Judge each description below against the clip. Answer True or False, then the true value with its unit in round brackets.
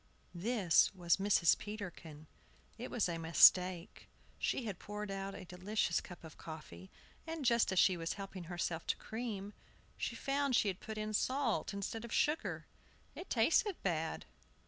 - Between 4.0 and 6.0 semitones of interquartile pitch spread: True (4.6 semitones)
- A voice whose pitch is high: True (195 Hz)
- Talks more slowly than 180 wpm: True (160 wpm)